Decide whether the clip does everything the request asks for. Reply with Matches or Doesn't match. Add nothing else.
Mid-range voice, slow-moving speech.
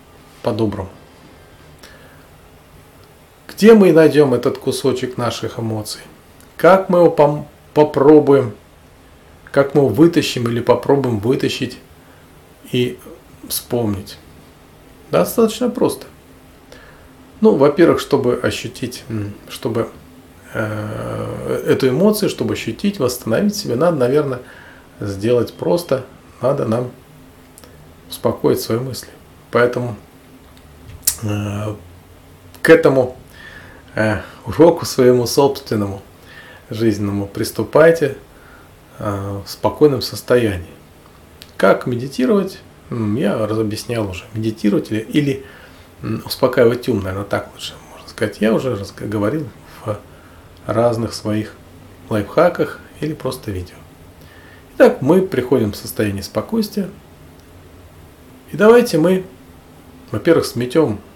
Doesn't match